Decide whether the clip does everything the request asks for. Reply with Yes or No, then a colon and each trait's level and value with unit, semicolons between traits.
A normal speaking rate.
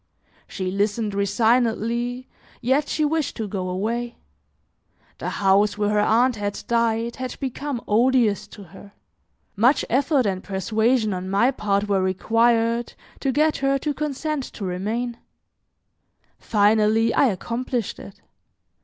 No: slow, 130 wpm